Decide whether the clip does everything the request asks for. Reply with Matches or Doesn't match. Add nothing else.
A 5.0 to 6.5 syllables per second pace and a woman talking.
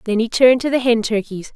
Matches